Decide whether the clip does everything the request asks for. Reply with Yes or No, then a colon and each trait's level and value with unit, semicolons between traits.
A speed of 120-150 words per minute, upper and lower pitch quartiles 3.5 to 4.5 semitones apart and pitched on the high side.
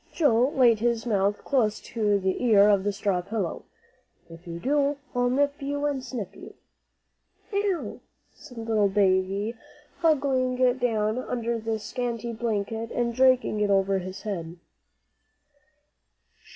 Yes: slow, 135 wpm; average, 4.0 semitones; high, 225 Hz